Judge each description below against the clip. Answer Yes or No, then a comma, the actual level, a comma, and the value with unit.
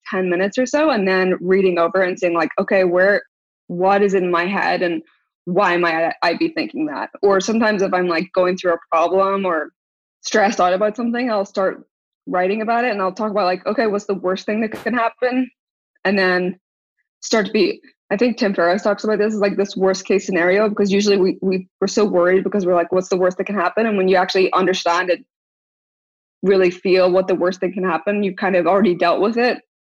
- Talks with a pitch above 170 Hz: Yes, high, 190 Hz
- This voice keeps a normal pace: No, fast, 225 wpm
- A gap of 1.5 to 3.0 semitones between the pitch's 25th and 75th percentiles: Yes, narrow, 2.6 semitones